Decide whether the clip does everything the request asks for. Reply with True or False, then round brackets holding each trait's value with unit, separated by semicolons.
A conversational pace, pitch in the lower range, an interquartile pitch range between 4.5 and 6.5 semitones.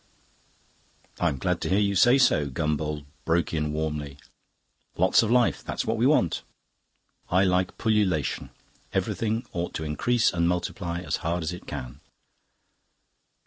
True (145 wpm; 85 Hz; 5.3 semitones)